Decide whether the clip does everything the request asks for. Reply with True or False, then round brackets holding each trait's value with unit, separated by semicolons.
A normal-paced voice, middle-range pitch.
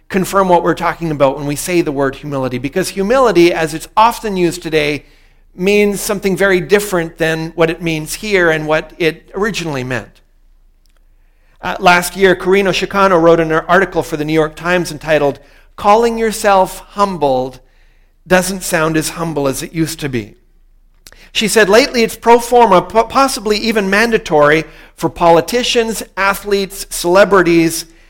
True (150 wpm; 170 Hz)